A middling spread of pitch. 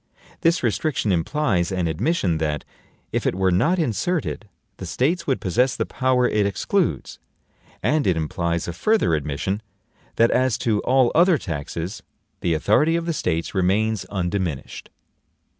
No: wide, 7.6 semitones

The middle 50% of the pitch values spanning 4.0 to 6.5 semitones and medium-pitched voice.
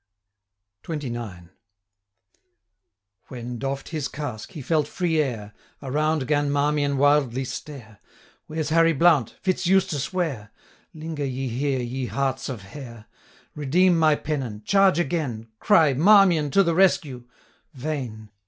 Yes: average, 4.4 semitones; medium, 145 Hz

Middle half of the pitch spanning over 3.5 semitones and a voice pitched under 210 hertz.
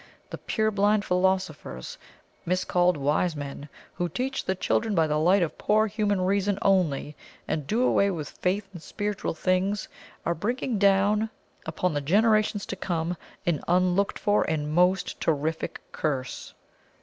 Yes: average, 4.1 semitones; medium, 185 Hz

